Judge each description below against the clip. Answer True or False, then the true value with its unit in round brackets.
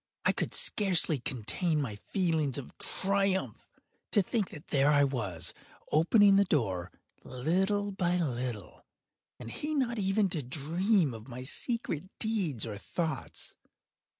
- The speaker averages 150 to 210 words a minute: False (135 wpm)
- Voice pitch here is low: False (160 Hz)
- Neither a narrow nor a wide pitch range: False (7.3 semitones)